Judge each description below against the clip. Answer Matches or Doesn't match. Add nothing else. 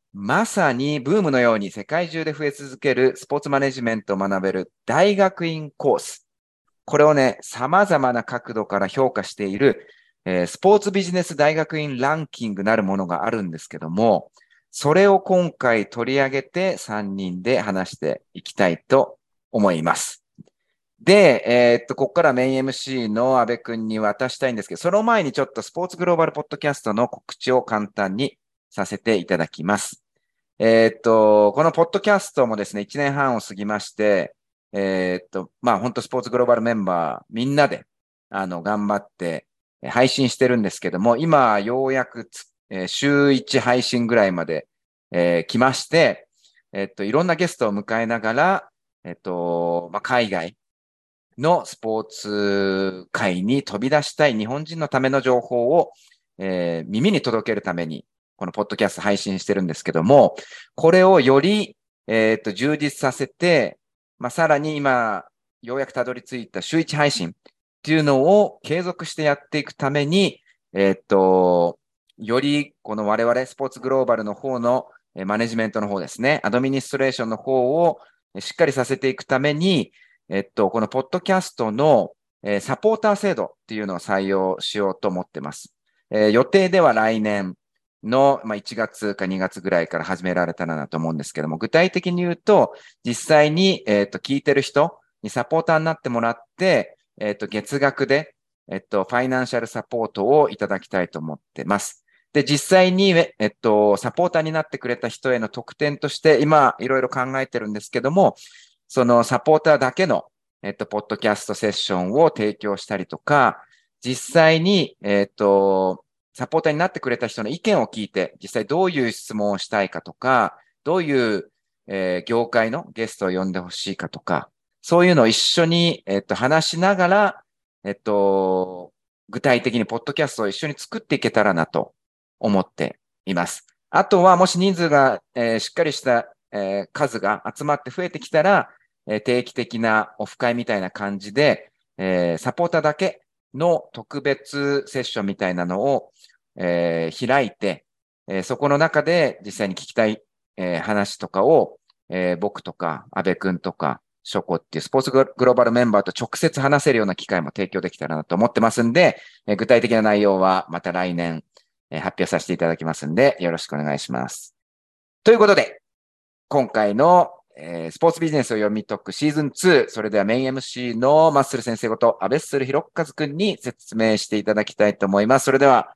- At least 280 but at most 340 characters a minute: Doesn't match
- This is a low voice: Matches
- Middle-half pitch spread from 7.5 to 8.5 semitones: Doesn't match